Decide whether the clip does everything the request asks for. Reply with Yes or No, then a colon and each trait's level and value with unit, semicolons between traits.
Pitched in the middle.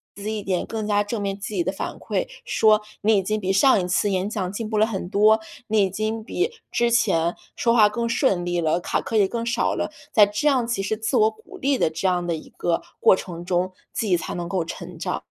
No: high, 205 Hz